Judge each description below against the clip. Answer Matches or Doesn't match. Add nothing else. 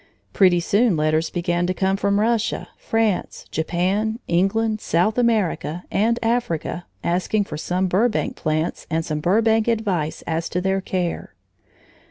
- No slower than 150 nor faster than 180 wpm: Doesn't match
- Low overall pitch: Doesn't match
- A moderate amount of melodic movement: Matches